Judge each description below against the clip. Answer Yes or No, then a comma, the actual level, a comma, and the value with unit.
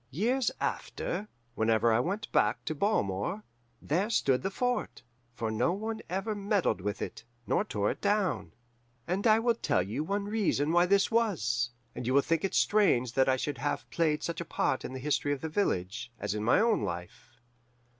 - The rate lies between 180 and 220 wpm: Yes, average, 195 wpm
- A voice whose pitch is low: No, medium, 160 Hz